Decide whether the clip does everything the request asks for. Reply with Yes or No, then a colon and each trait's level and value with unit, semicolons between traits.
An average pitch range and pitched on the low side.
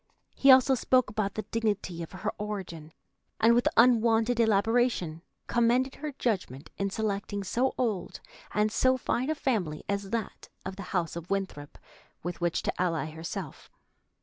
No: average, 4.8 semitones; high, 210 Hz